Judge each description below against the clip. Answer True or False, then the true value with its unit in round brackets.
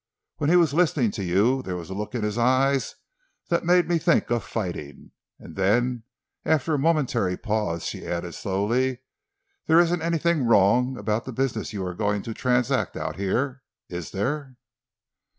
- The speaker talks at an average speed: True (170 wpm)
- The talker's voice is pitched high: False (120 Hz)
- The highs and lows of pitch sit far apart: True (5.7 semitones)